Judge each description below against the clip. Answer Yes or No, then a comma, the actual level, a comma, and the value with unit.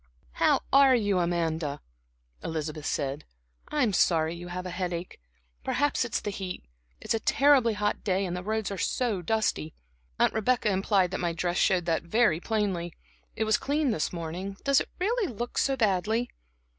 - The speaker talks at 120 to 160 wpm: No, average, 170 wpm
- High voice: Yes, high, 195 Hz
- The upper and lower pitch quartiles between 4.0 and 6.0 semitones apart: Yes, average, 4.8 semitones